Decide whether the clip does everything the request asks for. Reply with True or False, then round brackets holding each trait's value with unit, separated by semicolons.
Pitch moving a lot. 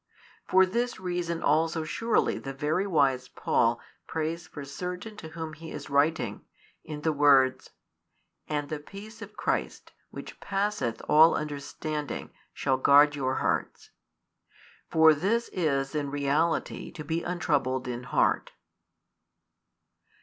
False (3.4 semitones)